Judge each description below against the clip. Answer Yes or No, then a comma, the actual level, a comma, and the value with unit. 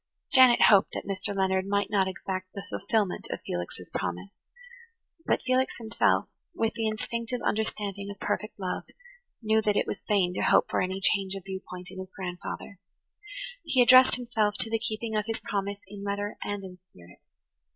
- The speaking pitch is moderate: No, high, 200 Hz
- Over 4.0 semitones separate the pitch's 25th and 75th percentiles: No, narrow, 2.6 semitones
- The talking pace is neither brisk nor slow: Yes, average, 175 wpm